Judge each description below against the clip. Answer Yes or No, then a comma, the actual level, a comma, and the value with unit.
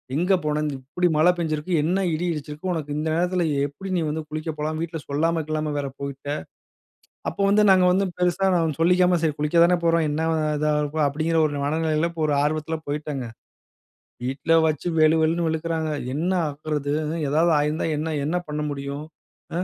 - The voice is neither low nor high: Yes, medium, 155 Hz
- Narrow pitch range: Yes, narrow, 2.1 semitones